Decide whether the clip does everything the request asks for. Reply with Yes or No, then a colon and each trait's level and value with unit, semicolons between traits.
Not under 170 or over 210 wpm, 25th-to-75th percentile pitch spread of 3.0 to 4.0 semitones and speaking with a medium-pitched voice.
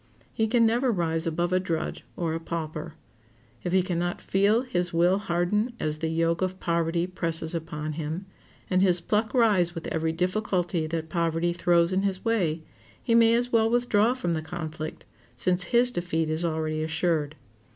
Yes: average, 180 wpm; average, 3.3 semitones; medium, 175 Hz